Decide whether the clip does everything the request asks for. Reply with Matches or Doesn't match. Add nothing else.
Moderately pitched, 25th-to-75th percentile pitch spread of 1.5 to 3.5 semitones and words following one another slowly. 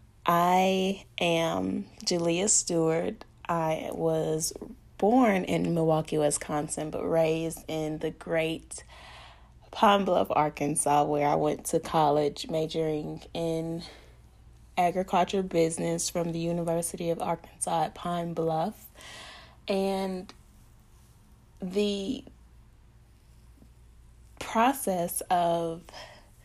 Matches